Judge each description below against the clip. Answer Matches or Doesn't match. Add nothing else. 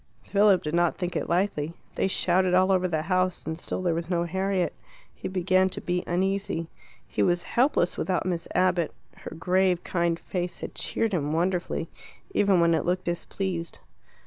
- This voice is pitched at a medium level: Matches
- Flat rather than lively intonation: Matches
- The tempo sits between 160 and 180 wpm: Matches